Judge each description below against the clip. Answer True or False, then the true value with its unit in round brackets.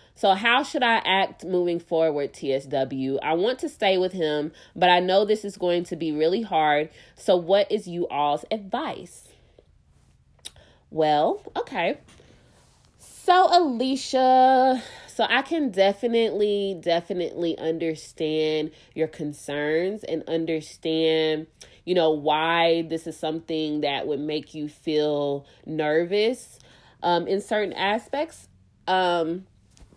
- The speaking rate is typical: False (120 wpm)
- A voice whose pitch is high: False (165 Hz)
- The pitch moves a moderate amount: True (5.0 semitones)